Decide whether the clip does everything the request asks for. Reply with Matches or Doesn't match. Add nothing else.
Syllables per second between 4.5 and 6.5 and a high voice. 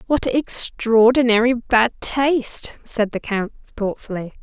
Doesn't match